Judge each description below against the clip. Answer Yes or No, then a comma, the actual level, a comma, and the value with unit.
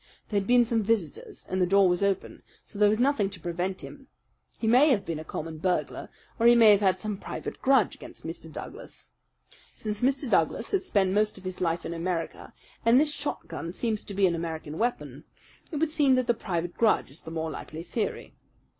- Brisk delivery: Yes, fast, 215 wpm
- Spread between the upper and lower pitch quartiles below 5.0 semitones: No, average, 5.3 semitones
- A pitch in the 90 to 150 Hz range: No, high, 200 Hz